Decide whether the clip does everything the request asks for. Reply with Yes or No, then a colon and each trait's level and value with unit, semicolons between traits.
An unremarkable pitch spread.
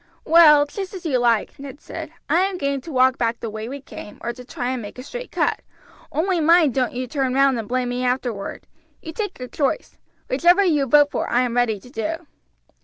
Yes: average, 4.5 semitones